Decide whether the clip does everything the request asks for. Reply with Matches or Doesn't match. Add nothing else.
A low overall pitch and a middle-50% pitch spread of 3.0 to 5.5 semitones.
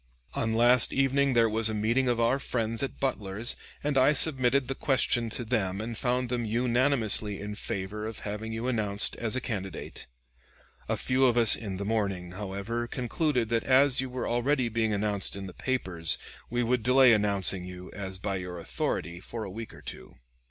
Matches